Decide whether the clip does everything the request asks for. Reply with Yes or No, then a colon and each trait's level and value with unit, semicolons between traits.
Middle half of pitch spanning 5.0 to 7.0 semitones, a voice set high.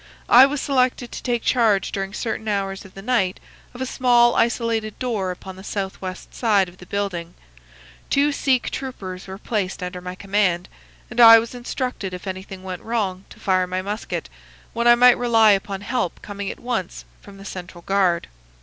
No: average, 4.2 semitones; high, 200 Hz